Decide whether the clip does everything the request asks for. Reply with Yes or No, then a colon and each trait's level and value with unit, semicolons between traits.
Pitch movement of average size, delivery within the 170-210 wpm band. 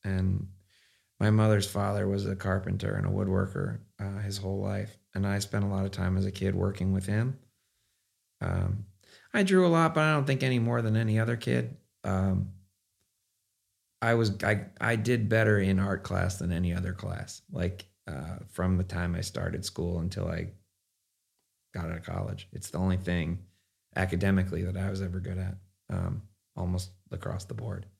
No: narrow, 2.1 semitones; average, 185 wpm